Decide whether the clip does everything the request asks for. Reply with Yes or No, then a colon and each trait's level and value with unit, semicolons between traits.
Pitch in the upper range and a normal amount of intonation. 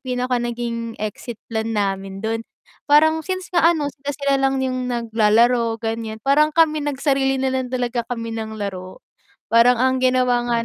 Yes: high, 245 Hz; average, 3.0 semitones